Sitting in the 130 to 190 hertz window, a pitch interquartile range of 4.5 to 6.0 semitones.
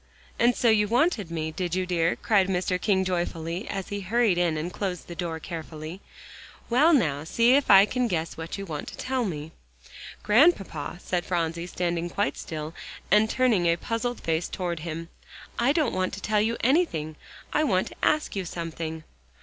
Yes: medium, 185 Hz; average, 5.1 semitones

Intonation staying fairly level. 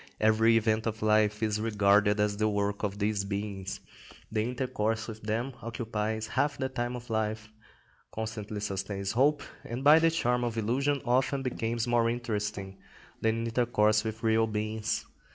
Yes: narrow, 2.1 semitones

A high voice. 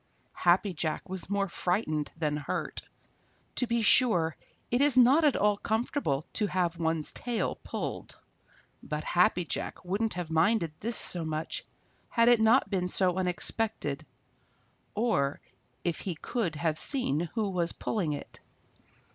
No: medium, 180 Hz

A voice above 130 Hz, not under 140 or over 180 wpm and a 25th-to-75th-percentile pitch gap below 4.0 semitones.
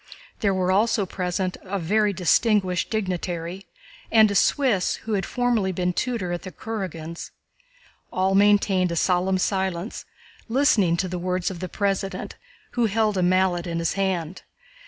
Yes: high, 190 Hz; average, 155 wpm; narrow, 2.5 semitones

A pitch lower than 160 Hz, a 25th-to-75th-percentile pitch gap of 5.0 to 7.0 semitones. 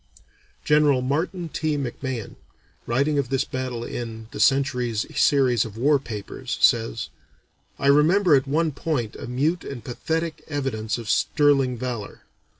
No: low, 135 Hz; average, 3.7 semitones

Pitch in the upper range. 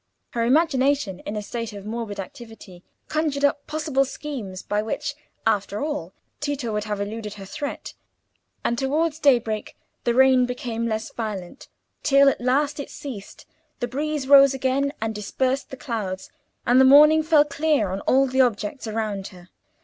Yes: very high, 250 Hz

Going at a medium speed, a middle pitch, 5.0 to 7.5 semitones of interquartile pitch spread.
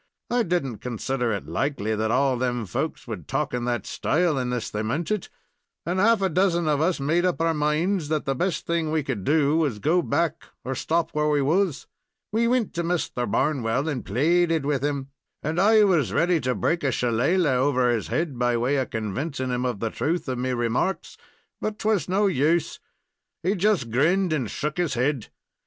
No: fast, 210 wpm; medium, 150 Hz; wide, 5.6 semitones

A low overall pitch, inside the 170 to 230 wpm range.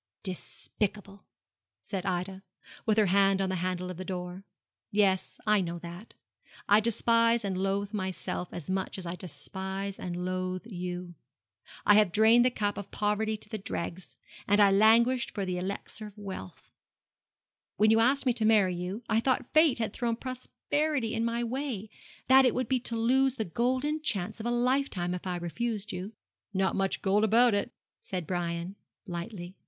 No: high, 205 Hz; average, 175 wpm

